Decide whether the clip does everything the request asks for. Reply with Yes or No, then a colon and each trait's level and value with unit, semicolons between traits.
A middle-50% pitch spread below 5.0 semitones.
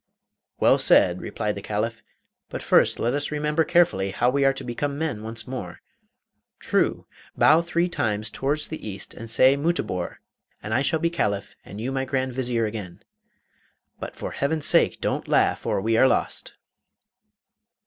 No: wide, 5.5 semitones